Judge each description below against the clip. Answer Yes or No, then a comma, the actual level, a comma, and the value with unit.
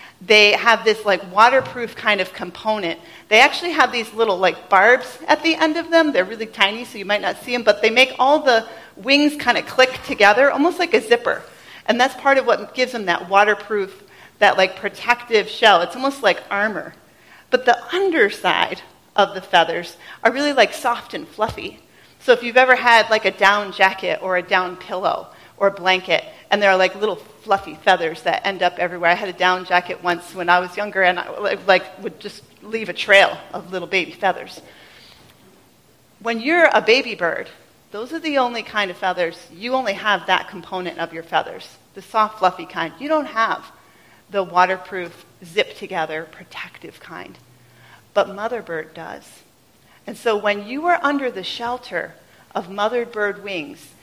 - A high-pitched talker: Yes, high, 205 Hz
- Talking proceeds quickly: No, average, 190 wpm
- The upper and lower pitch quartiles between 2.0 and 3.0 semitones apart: No, average, 4.6 semitones